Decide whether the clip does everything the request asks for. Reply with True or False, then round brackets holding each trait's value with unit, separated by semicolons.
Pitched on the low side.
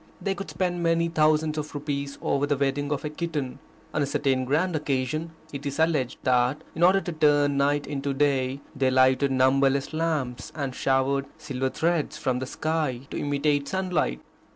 False (145 Hz)